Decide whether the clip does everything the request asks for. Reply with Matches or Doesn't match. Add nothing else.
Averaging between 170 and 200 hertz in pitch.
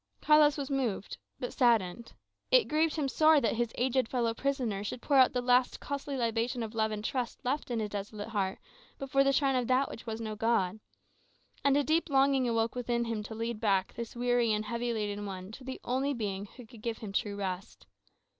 Doesn't match